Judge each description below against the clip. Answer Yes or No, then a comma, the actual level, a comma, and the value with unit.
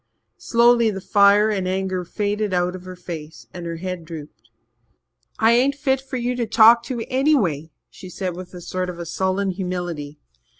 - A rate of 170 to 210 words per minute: Yes, average, 175 wpm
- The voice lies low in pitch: No, high, 190 Hz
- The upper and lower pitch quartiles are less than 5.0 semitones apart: Yes, average, 4.3 semitones